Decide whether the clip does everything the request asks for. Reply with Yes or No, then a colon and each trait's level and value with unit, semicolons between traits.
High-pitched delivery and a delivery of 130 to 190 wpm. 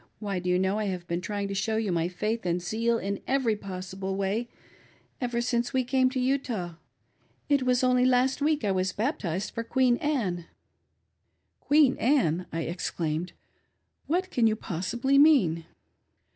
Yes: high, 220 Hz; average, 160 wpm